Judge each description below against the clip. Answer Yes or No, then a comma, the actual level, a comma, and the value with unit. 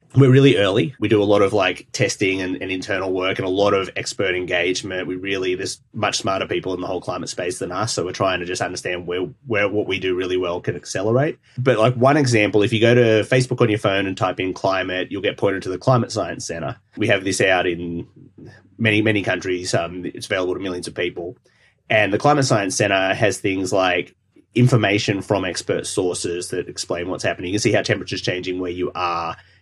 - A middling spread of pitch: Yes, average, 3.4 semitones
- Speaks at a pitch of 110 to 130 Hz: No, very low, 95 Hz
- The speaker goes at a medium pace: No, fast, 225 wpm